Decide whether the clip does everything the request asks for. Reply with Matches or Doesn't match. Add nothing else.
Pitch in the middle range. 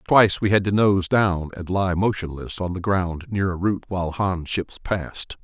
Doesn't match